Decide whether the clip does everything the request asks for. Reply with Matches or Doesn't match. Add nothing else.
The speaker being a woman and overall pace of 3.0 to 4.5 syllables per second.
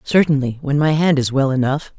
Doesn't match